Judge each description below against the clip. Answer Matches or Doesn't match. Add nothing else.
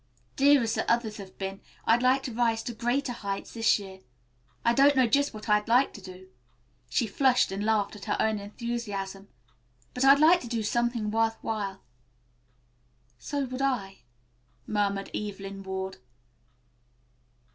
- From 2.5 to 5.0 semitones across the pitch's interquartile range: Matches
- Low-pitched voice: Doesn't match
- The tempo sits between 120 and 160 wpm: Matches